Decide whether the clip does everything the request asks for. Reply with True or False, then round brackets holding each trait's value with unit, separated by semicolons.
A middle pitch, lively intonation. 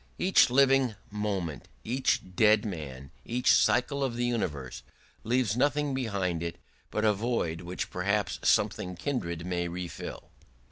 False (105 Hz; 6.1 semitones)